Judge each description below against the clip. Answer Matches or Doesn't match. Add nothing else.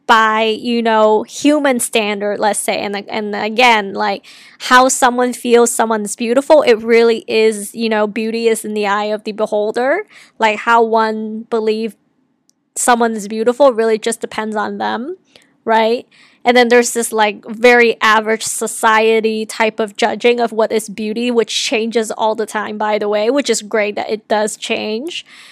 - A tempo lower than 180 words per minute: Matches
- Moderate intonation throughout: Doesn't match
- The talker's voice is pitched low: Doesn't match